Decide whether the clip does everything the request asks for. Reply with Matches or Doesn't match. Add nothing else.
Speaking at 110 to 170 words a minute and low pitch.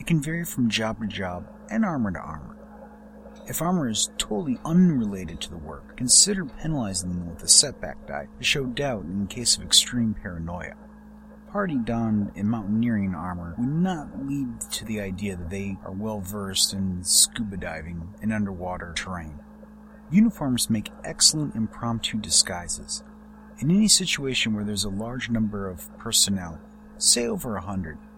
Matches